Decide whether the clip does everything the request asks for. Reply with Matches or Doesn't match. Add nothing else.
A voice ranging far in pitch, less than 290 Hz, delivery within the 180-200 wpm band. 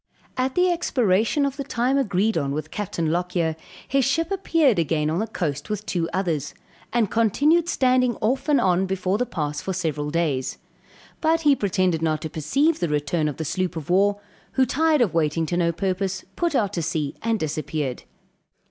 Matches